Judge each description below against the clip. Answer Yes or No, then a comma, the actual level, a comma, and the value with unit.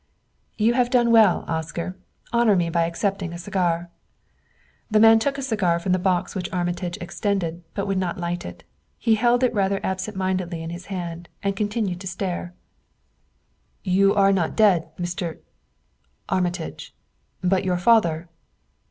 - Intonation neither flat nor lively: Yes, average, 3.0 semitones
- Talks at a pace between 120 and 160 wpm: Yes, average, 155 wpm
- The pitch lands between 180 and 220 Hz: Yes, medium, 185 Hz